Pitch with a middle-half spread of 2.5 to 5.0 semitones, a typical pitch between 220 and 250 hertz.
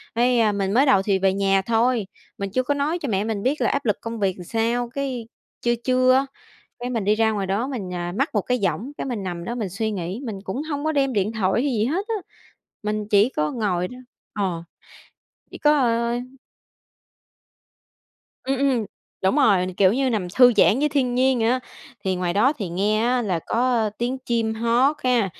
Yes: average, 4.3 semitones; high, 230 Hz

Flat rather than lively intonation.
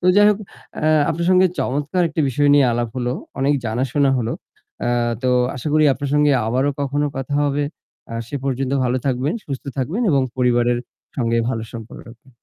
No: average, 3.1 semitones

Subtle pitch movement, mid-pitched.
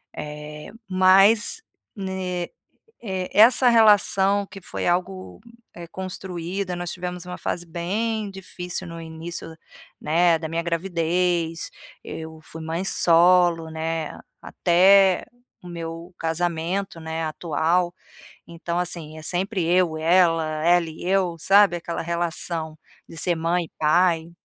Yes: narrow, 2.2 semitones; medium, 175 Hz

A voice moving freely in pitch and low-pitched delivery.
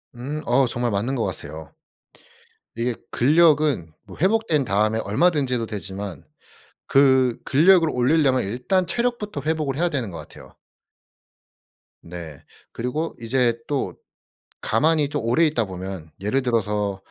Yes: wide, 6.4 semitones; low, 125 Hz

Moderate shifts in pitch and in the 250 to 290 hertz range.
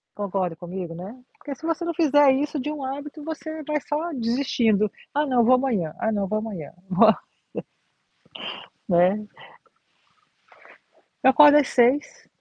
No: wide, 6.4 semitones; very high, 255 Hz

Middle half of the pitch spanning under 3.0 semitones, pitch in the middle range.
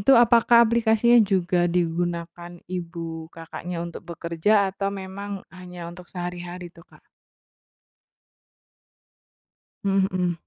Yes: narrow, 2.6 semitones; medium, 180 Hz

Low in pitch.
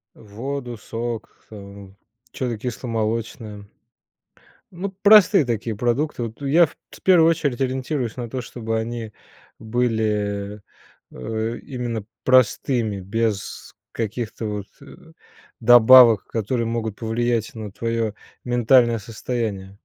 Yes: low, 115 Hz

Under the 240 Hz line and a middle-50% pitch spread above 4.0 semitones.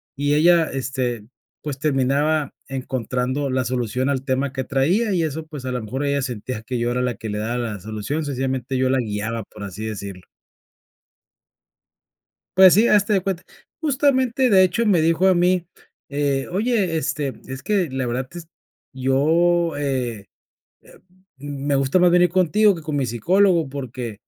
Yes: medium, 140 Hz; wide, 5.4 semitones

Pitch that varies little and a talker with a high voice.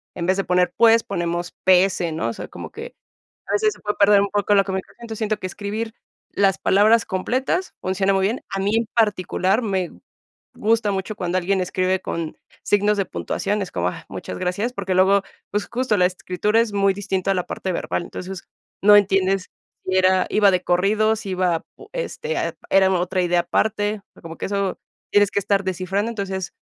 Yes: narrow, 2.3 semitones; high, 195 Hz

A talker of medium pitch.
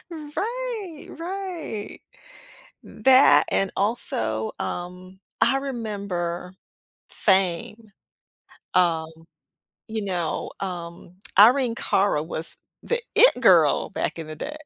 No: high, 200 Hz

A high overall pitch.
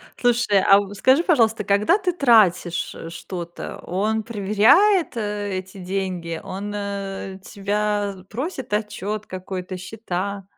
Yes: high, 205 Hz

